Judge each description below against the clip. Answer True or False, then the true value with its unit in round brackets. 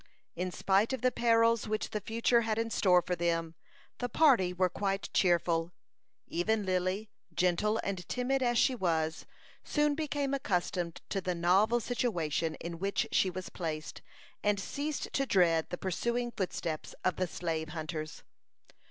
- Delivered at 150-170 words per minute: True (155 wpm)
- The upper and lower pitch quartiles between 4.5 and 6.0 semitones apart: True (5.0 semitones)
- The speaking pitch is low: False (190 Hz)